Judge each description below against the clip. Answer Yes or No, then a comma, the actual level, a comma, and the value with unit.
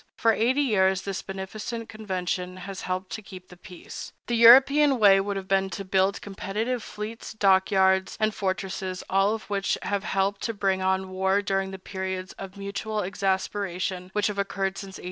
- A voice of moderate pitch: No, high, 195 Hz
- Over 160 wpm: Yes, average, 185 wpm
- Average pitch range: No, narrow, 1.8 semitones